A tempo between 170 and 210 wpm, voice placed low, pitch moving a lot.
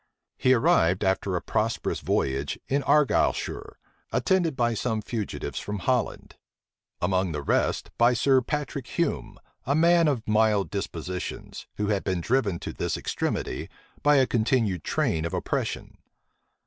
No: average, 140 wpm; low, 110 Hz; wide, 5.8 semitones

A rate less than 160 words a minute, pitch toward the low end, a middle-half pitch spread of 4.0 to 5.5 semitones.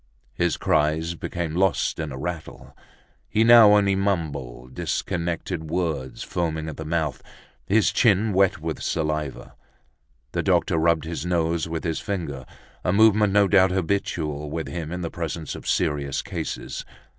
No: average, 150 wpm; very low, 85 Hz; average, 3.5 semitones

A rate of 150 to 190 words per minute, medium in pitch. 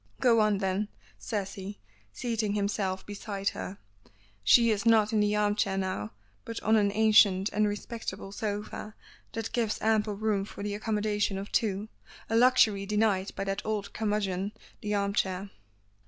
No: average, 160 wpm; high, 205 Hz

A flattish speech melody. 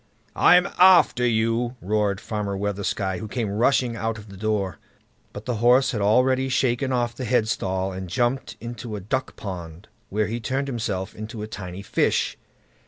No: average, 3.5 semitones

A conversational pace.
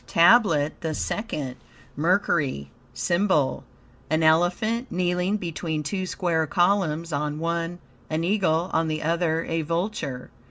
No: slow, 120 wpm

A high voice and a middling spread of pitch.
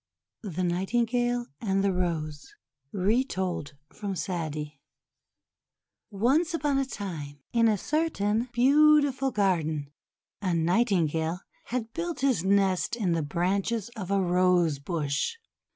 No: high, 195 Hz; wide, 5.9 semitones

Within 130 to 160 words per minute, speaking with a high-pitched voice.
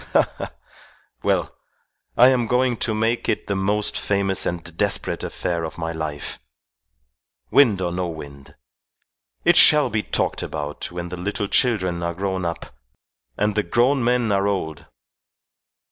No: average, 150 wpm; very low, 95 Hz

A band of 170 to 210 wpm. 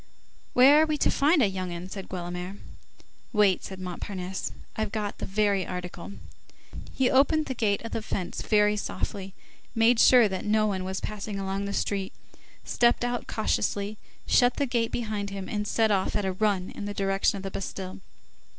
Yes: average, 185 wpm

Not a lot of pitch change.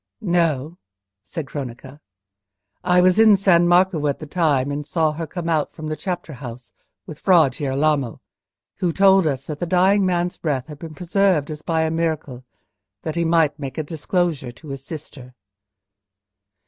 No: average, 3.6 semitones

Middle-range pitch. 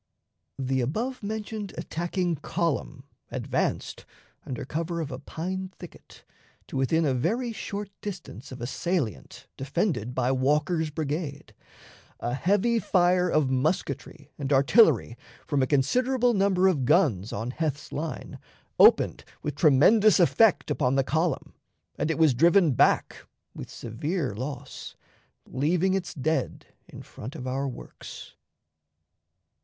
Yes: medium, 155 Hz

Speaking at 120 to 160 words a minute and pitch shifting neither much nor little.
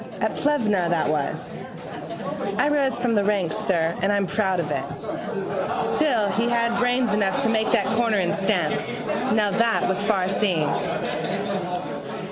Yes: average, 145 wpm; average, 4.0 semitones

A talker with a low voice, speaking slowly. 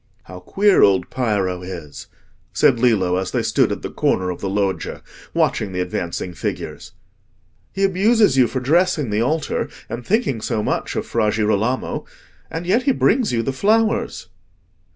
No: low, 115 Hz; average, 165 wpm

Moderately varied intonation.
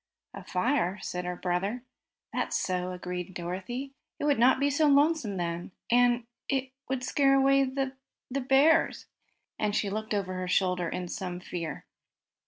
No: wide, 6.9 semitones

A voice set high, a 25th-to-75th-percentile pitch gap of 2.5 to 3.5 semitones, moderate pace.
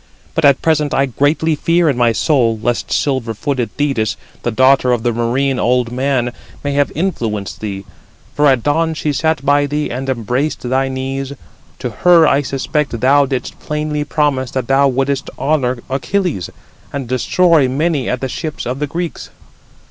No: low, 135 Hz; average, 3.0 semitones; average, 170 wpm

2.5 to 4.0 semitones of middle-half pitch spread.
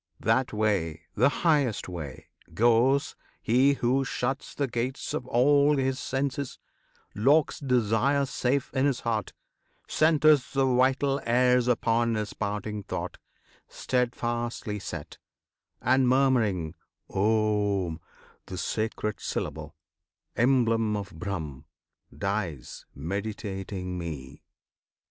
No: average, 4.7 semitones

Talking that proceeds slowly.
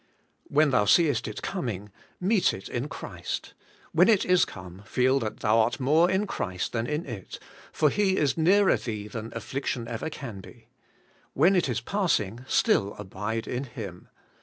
No: average, 170 wpm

